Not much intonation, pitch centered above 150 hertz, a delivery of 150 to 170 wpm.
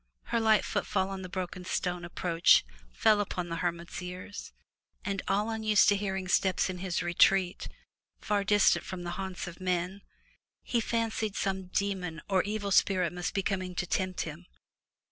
Yes: narrow, 2.1 semitones; high, 190 Hz; average, 165 wpm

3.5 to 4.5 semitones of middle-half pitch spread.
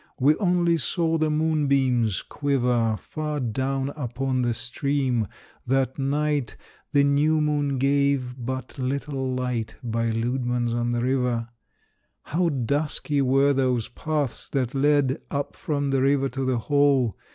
No: average, 2.7 semitones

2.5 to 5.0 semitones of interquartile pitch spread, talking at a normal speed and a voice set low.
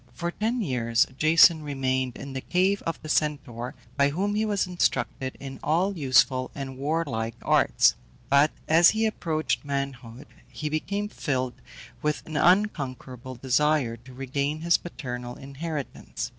No: average, 4.4 semitones; average, 145 wpm; medium, 145 Hz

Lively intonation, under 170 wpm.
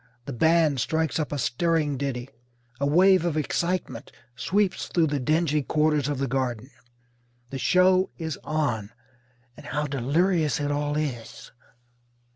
No: average, 3.3 semitones; average, 140 wpm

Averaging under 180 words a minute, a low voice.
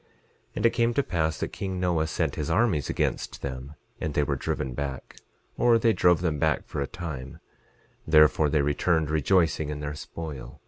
No: average, 190 wpm; very low, 80 Hz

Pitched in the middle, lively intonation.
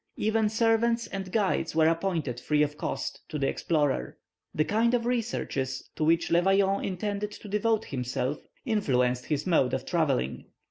Yes: medium, 175 Hz; wide, 6.5 semitones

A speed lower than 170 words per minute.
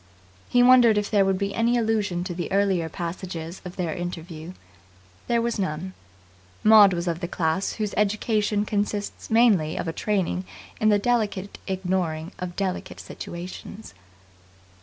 Yes: average, 150 wpm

